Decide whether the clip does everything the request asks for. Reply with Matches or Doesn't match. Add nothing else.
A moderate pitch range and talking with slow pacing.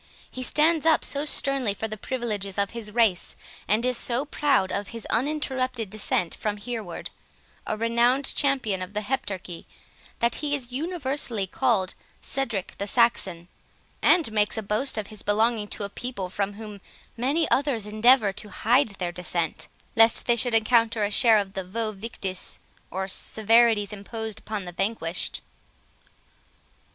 Doesn't match